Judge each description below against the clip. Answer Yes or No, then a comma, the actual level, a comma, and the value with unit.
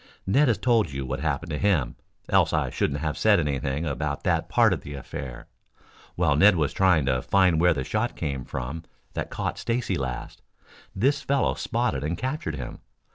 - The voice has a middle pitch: No, very low, 80 Hz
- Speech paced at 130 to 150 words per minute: No, average, 185 wpm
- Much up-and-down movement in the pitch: Yes, wide, 6.8 semitones